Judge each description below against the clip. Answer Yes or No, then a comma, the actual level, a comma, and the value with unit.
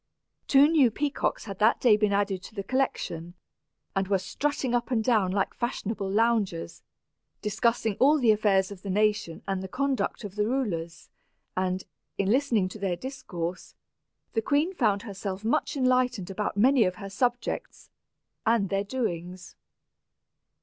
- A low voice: No, high, 210 Hz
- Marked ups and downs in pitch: No, average, 4.4 semitones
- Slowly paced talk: No, average, 155 wpm